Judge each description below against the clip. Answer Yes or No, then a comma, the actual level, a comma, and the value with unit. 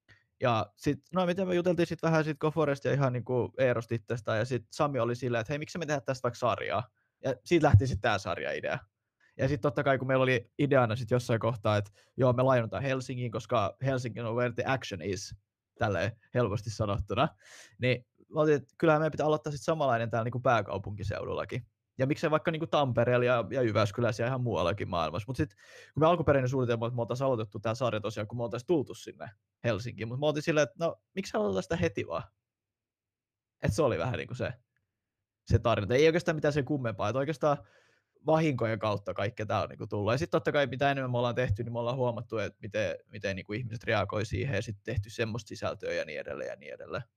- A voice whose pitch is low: Yes, low, 125 Hz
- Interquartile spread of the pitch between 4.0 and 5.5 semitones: Yes, average, 4.7 semitones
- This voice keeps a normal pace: No, fast, 215 wpm